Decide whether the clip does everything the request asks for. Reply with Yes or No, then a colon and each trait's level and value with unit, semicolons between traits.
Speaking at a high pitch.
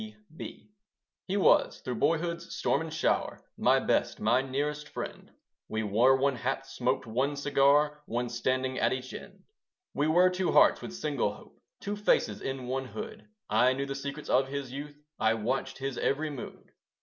No: medium, 140 Hz